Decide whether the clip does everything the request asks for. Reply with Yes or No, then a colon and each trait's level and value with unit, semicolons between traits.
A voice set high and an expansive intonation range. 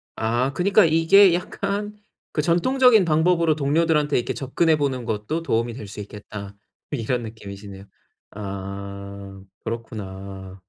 No: low, 120 Hz; wide, 8.6 semitones